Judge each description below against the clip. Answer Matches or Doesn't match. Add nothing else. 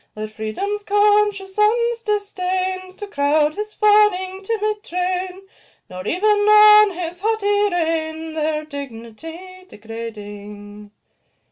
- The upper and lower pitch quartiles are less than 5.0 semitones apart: Doesn't match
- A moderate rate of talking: Doesn't match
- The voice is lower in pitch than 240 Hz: Doesn't match